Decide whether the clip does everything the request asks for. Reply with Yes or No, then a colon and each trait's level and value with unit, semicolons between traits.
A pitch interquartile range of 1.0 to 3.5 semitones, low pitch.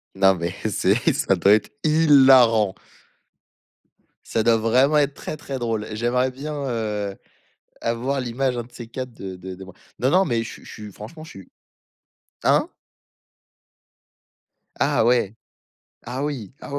No: average, 4.1 semitones; low, 120 Hz